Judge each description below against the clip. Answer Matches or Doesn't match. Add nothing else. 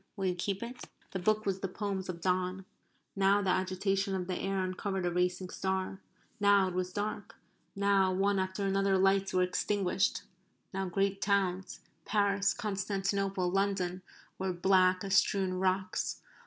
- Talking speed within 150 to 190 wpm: Matches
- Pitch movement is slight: Matches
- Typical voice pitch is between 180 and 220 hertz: Matches